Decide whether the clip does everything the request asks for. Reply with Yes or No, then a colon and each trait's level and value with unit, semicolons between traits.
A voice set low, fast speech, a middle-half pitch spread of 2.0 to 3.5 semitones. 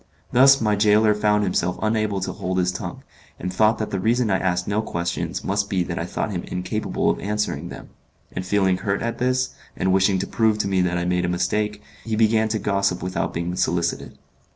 Yes: low, 100 Hz; fast, 215 wpm; average, 2.9 semitones